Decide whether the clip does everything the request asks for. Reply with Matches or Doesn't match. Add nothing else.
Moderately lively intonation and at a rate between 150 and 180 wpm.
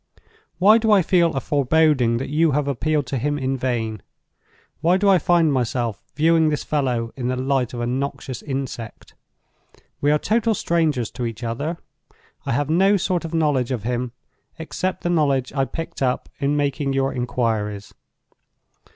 Matches